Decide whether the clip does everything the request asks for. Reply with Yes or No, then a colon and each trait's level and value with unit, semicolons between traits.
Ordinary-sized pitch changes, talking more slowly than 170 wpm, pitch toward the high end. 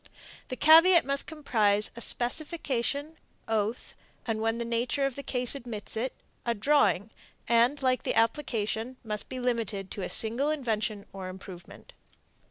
Yes: average, 4.2 semitones; average, 155 wpm; high, 235 Hz